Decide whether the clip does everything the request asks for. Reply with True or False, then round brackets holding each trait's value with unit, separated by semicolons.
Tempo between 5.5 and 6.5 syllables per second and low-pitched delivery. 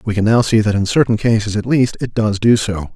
True (5.9 syllables/s; 110 Hz)